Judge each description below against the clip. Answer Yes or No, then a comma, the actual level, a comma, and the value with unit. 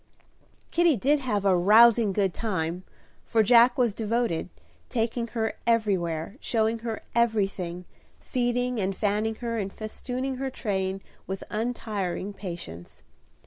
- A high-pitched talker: Yes, high, 220 Hz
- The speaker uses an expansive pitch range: No, average, 3.7 semitones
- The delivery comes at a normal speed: No, slow, 125 wpm